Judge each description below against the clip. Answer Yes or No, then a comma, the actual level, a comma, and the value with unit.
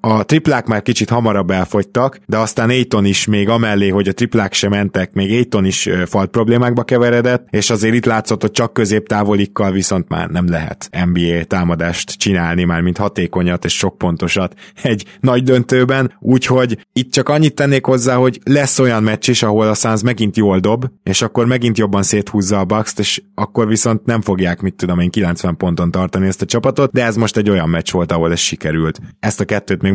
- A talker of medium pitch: No, low, 105 Hz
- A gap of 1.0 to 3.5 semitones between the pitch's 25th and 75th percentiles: No, average, 4.1 semitones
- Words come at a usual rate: No, fast, 200 wpm